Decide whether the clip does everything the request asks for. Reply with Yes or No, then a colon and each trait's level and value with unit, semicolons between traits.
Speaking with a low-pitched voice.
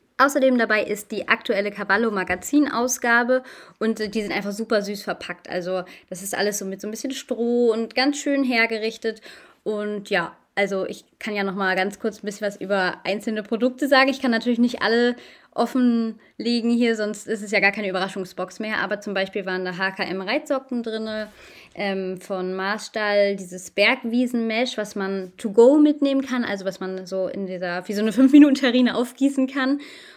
No: high, 215 Hz